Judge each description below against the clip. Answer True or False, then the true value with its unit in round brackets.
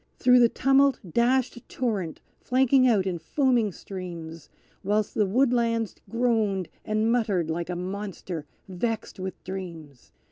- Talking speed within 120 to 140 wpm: True (135 wpm)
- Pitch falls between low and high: False (210 Hz)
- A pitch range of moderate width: True (5.0 semitones)